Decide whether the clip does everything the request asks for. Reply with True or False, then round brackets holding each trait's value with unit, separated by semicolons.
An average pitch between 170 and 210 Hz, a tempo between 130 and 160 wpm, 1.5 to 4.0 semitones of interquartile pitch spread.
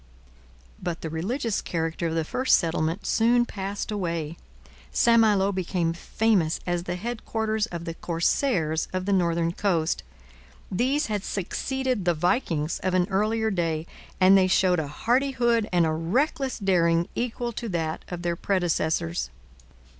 False (185 Hz; 145 wpm; 4.9 semitones)